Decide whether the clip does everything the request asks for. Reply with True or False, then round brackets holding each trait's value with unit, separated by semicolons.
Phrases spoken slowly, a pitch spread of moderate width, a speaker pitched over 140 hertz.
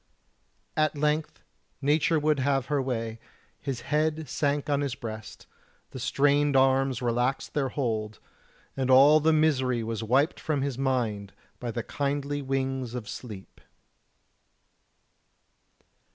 False (125 wpm; 3.0 semitones; 135 Hz)